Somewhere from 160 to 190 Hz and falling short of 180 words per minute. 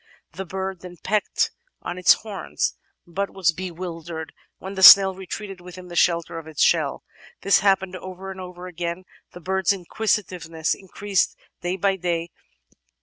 Yes: medium, 185 Hz; average, 150 wpm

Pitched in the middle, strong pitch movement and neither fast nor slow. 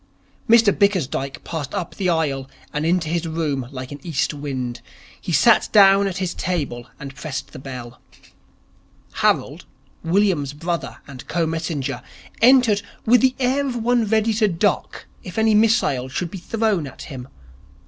Yes: medium, 170 Hz; wide, 6.9 semitones; average, 160 wpm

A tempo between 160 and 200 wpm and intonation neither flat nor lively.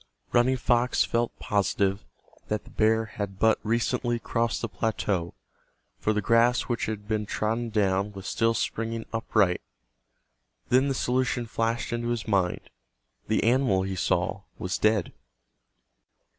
No: slow, 135 wpm; average, 3.1 semitones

